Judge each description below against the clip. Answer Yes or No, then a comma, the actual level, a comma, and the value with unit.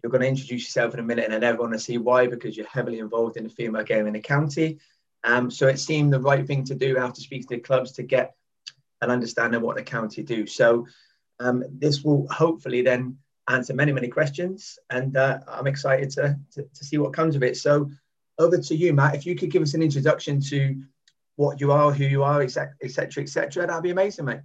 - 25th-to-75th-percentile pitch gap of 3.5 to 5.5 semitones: No, average, 2.9 semitones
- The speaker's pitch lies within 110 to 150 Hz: Yes, low, 135 Hz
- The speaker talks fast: Yes, fast, 245 wpm